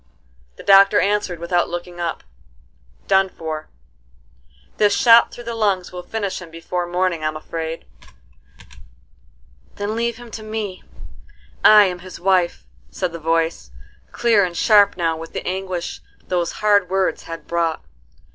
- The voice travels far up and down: No, average, 3.2 semitones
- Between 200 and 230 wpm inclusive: No, average, 145 wpm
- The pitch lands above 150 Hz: Yes, medium, 185 Hz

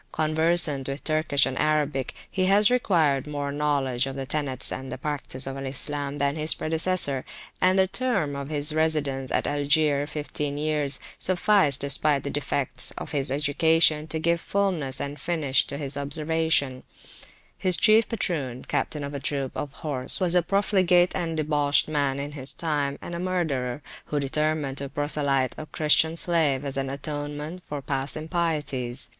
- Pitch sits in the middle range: Yes, medium, 145 Hz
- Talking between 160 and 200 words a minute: Yes, average, 165 wpm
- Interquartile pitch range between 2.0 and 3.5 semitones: Yes, narrow, 2.6 semitones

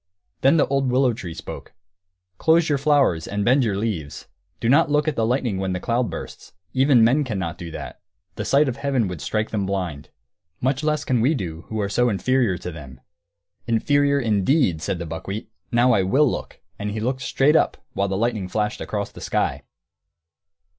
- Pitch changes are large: Yes, wide, 5.9 semitones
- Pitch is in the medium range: No, low, 115 Hz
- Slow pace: No, average, 195 wpm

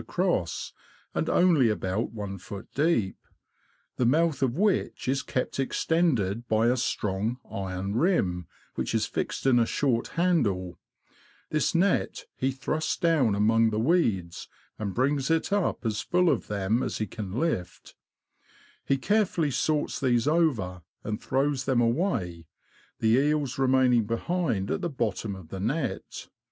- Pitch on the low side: Yes, low, 125 Hz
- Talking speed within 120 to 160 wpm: Yes, average, 150 wpm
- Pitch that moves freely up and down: Yes, wide, 6.8 semitones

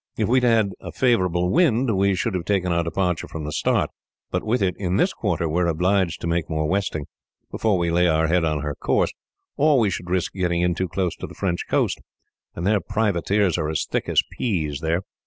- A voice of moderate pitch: No, very low, 90 Hz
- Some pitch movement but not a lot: Yes, average, 3.3 semitones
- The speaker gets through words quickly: Yes, fast, 230 wpm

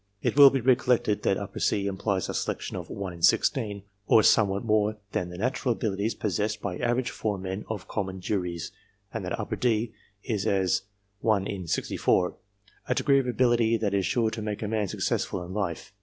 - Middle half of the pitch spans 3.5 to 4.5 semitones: No, average, 2.9 semitones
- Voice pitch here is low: Yes, low, 105 Hz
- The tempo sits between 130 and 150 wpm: No, average, 185 wpm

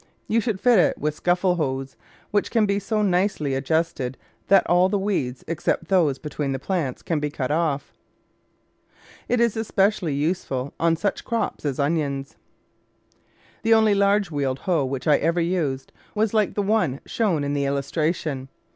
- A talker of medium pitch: Yes, medium, 165 Hz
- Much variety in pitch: Yes, wide, 6.1 semitones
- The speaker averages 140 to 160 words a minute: No, average, 170 wpm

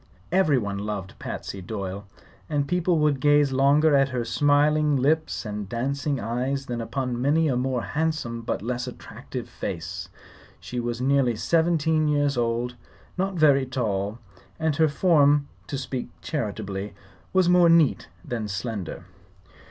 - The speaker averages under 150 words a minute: Yes, average, 140 wpm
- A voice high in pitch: No, low, 135 Hz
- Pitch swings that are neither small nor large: Yes, average, 4.5 semitones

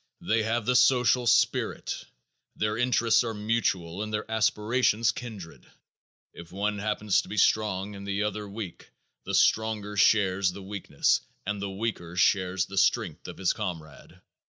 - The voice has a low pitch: Yes, low, 105 Hz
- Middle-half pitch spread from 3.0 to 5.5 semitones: No, narrow, 2.4 semitones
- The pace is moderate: Yes, average, 155 wpm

